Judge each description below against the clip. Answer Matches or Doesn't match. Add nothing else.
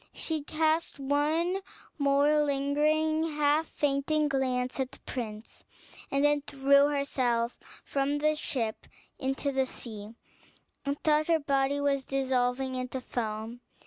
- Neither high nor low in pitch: Doesn't match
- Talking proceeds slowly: Matches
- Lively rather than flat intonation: Doesn't match